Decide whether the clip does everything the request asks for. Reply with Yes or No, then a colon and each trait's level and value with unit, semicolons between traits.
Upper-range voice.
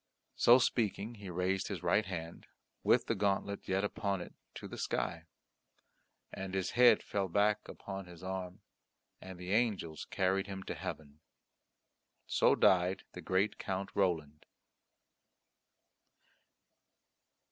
No: very low, 95 Hz